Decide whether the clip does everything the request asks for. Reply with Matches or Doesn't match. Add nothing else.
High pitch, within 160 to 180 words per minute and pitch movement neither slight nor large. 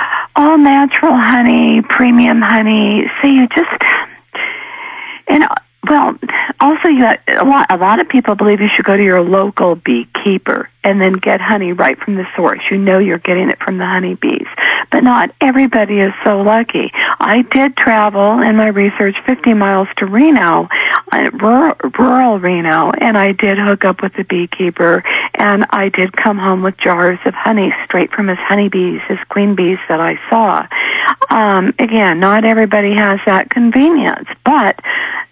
Matches